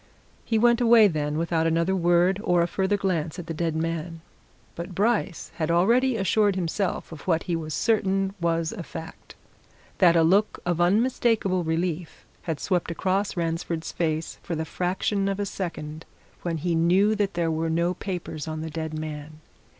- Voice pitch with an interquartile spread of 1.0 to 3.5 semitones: Yes, average, 3.1 semitones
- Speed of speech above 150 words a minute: Yes, average, 175 wpm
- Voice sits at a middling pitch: Yes, medium, 175 Hz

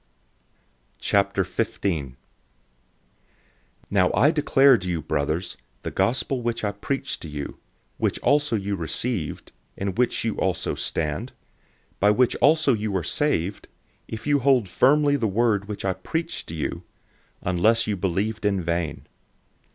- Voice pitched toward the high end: No, low, 100 Hz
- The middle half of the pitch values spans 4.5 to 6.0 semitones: Yes, wide, 5.4 semitones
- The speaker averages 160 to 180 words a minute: No, average, 145 wpm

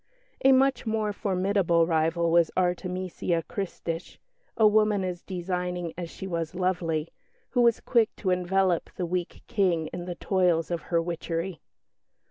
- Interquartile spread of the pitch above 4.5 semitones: No, narrow, 2.4 semitones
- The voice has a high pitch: No, medium, 180 Hz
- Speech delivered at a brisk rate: No, average, 145 wpm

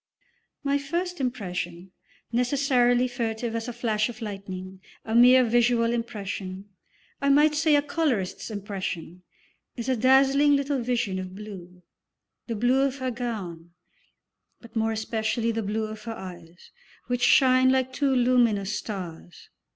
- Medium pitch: No, high, 230 Hz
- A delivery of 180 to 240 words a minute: No, average, 140 wpm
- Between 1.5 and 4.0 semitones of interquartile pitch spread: No, average, 4.4 semitones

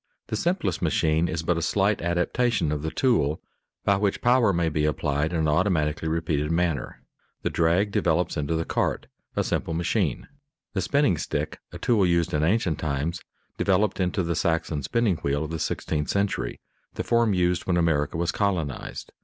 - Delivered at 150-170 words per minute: No, average, 180 wpm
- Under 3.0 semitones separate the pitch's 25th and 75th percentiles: No, average, 3.9 semitones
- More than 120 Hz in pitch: No, very low, 85 Hz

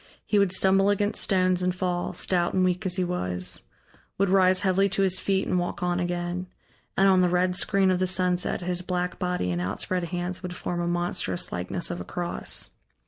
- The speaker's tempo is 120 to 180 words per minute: No, fast, 205 wpm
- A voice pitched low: No, medium, 180 Hz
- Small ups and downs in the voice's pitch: Yes, narrow, 1.1 semitones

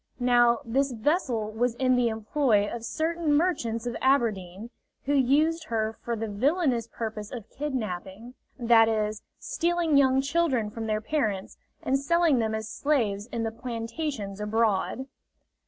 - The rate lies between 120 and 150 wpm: Yes, average, 145 wpm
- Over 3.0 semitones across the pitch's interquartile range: Yes, average, 4.2 semitones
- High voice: Yes, high, 235 Hz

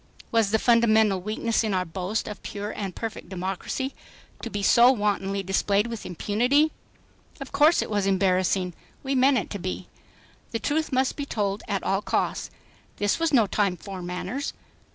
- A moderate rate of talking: Yes, average, 175 wpm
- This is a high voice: Yes, high, 210 Hz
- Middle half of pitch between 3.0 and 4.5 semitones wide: Yes, average, 3.8 semitones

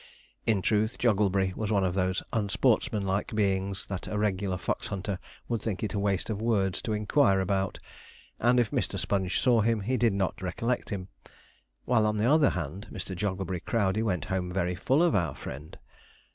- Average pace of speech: Yes, average, 180 wpm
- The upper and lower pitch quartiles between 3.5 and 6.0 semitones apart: No, average, 2.8 semitones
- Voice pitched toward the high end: No, low, 100 Hz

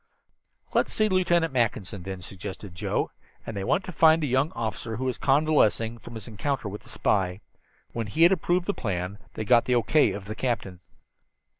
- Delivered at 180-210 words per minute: Yes, average, 195 wpm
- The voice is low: Yes, low, 115 Hz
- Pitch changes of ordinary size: No, wide, 7.0 semitones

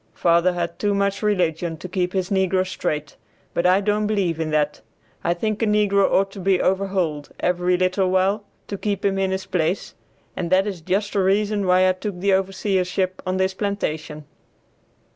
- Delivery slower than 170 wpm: No, average, 185 wpm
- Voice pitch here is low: No, high, 190 Hz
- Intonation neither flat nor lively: No, narrow, 2.0 semitones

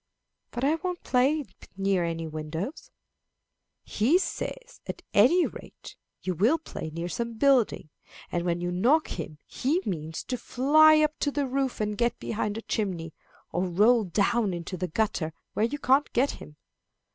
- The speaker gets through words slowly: No, average, 165 wpm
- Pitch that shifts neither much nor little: No, wide, 7.9 semitones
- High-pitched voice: Yes, high, 220 Hz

